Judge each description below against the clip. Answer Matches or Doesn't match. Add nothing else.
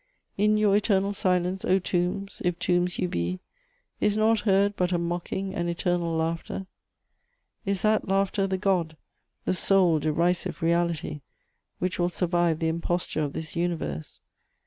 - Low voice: Doesn't match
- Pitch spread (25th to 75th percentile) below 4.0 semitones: Matches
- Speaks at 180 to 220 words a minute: Doesn't match